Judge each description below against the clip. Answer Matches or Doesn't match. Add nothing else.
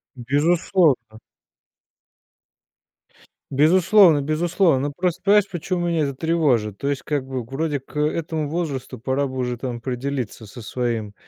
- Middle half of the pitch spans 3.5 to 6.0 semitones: Matches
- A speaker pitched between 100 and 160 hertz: Matches